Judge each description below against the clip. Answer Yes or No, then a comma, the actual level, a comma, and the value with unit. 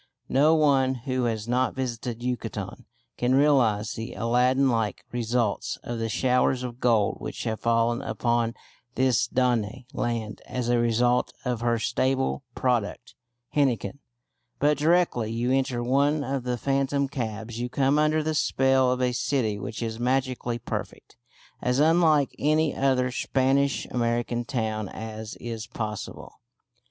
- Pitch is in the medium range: No, low, 125 Hz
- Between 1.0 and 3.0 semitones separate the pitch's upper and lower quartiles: Yes, narrow, 2.5 semitones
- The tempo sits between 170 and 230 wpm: No, average, 145 wpm